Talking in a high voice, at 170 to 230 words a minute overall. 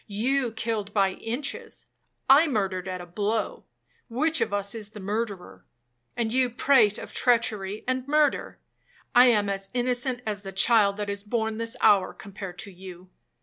No: high, 210 Hz; average, 150 wpm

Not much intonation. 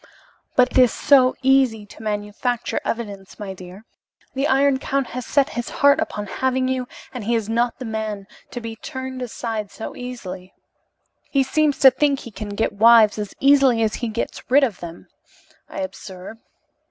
No: average, 3.8 semitones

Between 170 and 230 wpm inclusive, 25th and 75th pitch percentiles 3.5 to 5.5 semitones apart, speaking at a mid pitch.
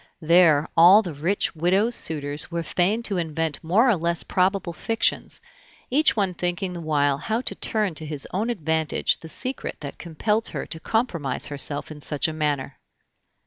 Yes: average, 175 wpm; average, 4.7 semitones; medium, 170 Hz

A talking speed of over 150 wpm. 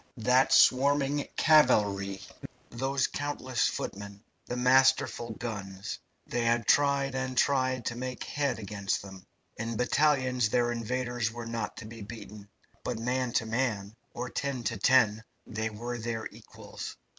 No: average, 140 wpm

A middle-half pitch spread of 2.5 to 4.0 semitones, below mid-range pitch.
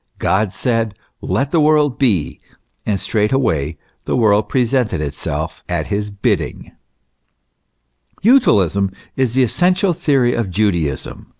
No: wide, 5.6 semitones; low, 110 Hz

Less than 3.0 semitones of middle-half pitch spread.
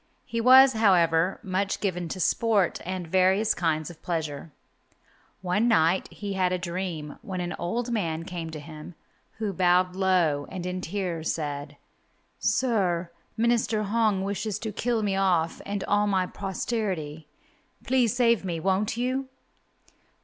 No: average, 4.0 semitones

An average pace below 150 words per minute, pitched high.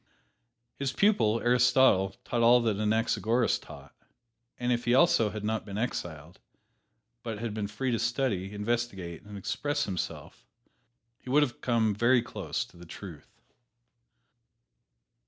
No: average, 140 wpm; low, 115 Hz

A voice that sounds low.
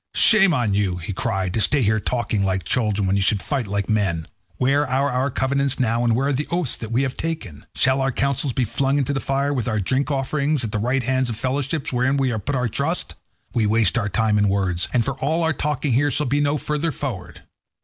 Yes: low, 130 Hz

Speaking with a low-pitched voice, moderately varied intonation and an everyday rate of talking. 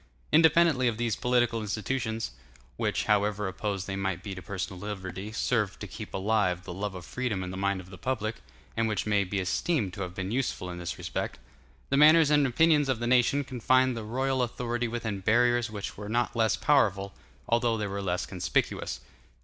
Yes: low, 110 Hz; average, 4.3 semitones; average, 190 wpm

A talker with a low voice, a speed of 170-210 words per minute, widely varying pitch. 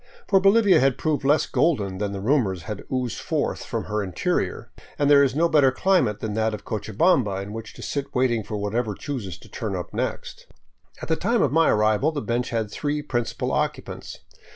Yes: low, 120 Hz; fast, 205 wpm; wide, 5.9 semitones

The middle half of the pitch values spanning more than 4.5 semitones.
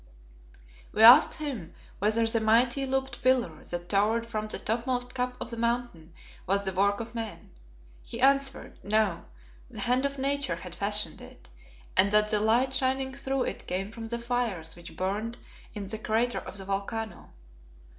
No: average, 3.6 semitones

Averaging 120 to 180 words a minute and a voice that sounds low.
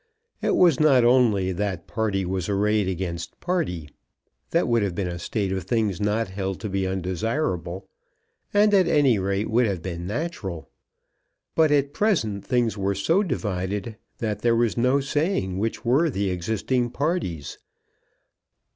Yes: average, 155 wpm; low, 105 Hz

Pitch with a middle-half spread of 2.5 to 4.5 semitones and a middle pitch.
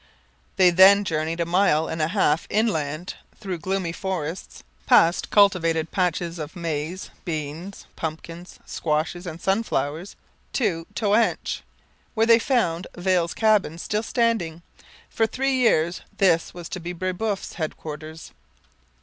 Yes: average, 3.5 semitones; medium, 175 Hz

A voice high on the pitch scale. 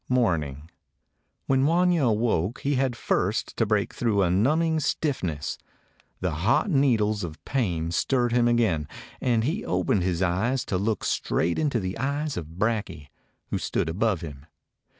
No: low, 110 Hz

